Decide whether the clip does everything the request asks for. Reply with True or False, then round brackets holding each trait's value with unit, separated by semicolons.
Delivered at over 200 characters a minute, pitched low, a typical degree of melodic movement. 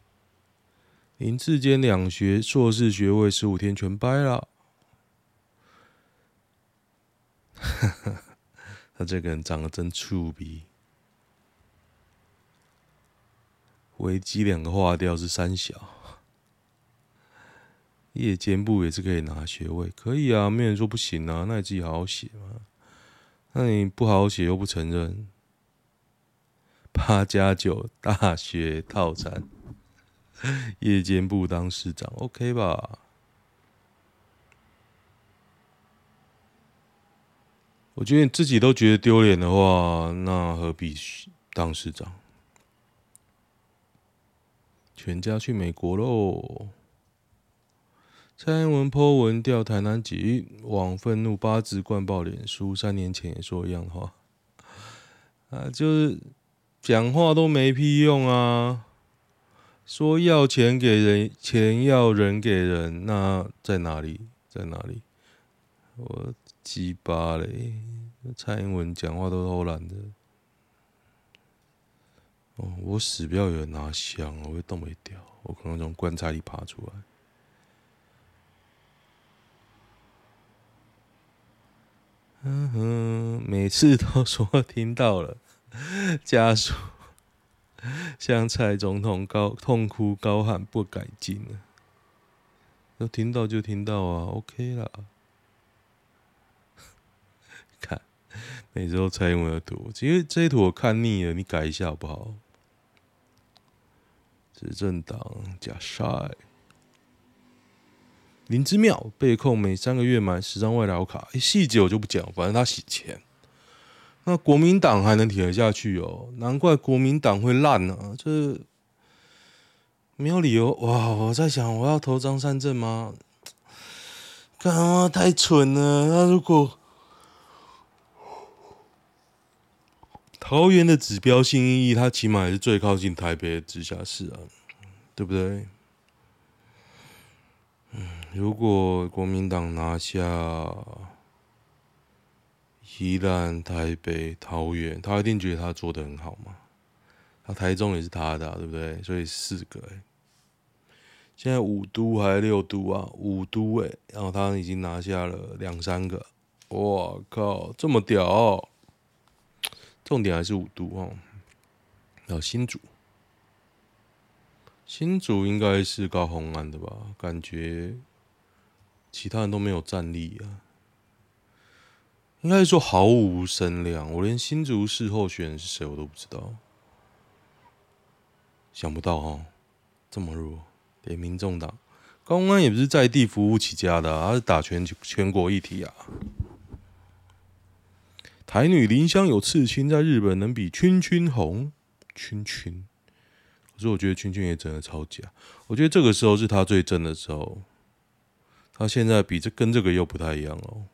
False (175 characters per minute; 105 Hz; 4.4 semitones)